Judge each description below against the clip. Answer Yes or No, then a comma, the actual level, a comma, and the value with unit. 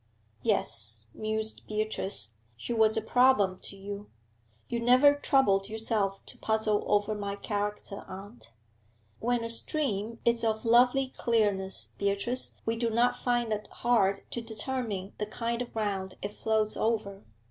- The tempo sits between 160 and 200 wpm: No, average, 145 wpm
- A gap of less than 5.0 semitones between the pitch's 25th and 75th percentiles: Yes, average, 2.8 semitones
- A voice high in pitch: Yes, high, 220 Hz